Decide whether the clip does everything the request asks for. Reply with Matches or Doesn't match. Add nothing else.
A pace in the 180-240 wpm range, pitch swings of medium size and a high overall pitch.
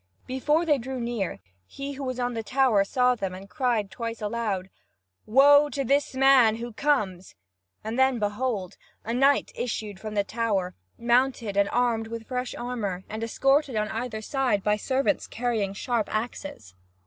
Doesn't match